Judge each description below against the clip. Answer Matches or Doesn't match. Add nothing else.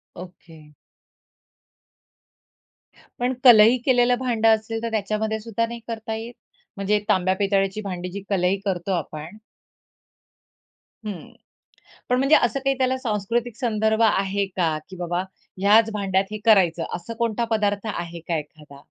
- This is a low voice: Doesn't match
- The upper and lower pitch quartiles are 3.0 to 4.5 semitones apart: Matches